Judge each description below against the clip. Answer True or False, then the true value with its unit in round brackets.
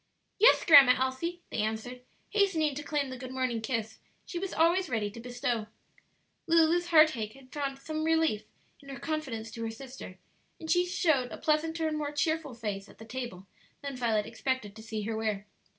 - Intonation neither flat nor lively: False (5.8 semitones)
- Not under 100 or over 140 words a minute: False (185 wpm)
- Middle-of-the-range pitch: False (260 Hz)